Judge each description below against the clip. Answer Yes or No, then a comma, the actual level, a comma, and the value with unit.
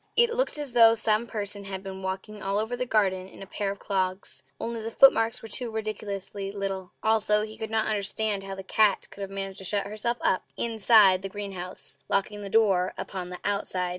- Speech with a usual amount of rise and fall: No, narrow, 2.2 semitones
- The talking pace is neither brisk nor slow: No, fast, 210 wpm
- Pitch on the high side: Yes, high, 205 Hz